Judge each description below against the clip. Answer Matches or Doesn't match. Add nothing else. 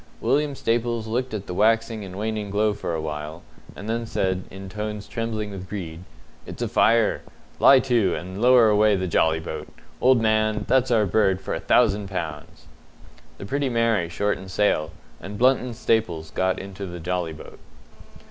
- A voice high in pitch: Doesn't match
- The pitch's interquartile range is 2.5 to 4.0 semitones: Matches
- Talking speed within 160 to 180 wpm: Matches